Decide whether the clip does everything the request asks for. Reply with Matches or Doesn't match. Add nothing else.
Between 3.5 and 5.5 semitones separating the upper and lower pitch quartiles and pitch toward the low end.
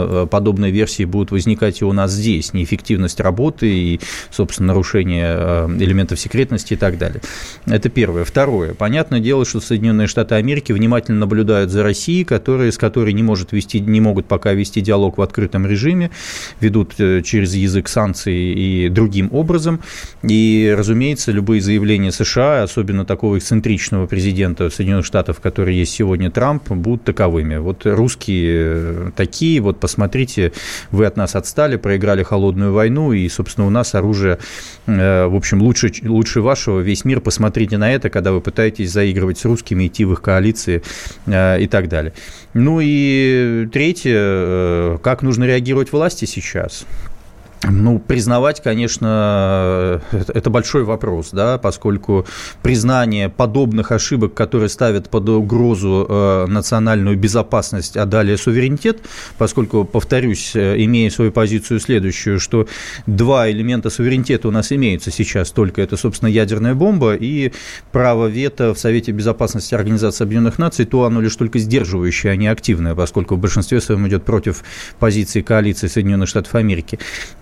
Doesn't match